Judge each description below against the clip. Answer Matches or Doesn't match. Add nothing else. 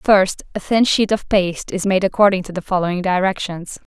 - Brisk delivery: Doesn't match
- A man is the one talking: Doesn't match